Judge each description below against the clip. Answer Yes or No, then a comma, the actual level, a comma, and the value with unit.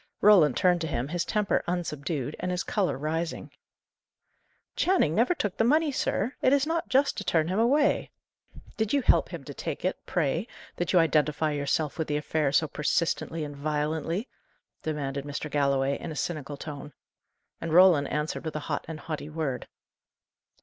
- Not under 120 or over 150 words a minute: No, average, 175 wpm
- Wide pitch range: No, average, 4.3 semitones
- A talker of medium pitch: Yes, medium, 160 Hz